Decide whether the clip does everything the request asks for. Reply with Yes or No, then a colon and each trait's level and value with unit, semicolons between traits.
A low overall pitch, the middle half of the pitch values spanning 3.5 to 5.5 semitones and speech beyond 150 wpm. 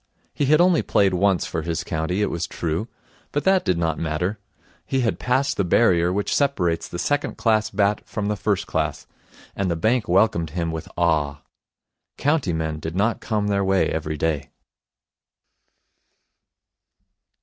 Yes: very low, 95 Hz; average, 5.0 semitones; average, 160 wpm